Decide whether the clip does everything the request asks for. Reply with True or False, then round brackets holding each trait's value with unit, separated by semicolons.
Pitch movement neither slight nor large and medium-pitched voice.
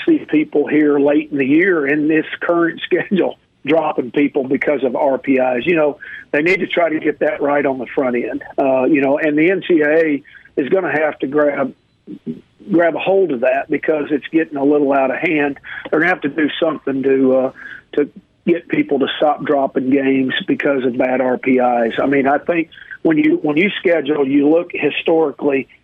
True (3.5 semitones; 145 Hz)